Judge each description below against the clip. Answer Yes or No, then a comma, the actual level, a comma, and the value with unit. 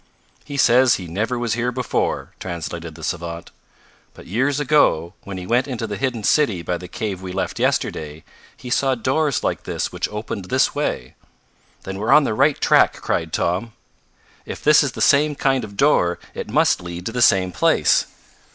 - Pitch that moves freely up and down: Yes, wide, 6.6 semitones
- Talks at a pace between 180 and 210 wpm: Yes, average, 190 wpm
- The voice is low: Yes, low, 105 Hz